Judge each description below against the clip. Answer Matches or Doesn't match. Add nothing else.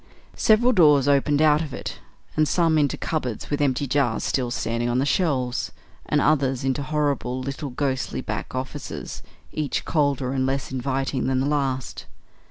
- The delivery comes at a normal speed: Matches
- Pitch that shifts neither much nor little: Doesn't match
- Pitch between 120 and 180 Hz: Matches